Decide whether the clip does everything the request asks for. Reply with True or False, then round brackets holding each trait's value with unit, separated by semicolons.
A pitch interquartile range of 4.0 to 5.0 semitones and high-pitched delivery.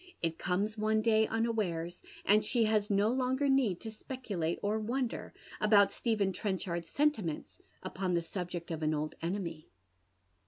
True (4.4 semitones; 205 Hz)